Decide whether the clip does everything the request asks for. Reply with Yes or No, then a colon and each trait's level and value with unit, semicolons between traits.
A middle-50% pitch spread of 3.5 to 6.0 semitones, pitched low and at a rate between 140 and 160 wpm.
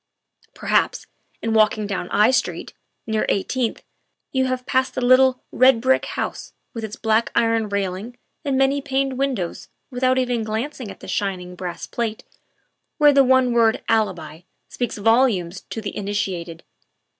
No: average, 4.2 semitones; high, 230 Hz; average, 155 wpm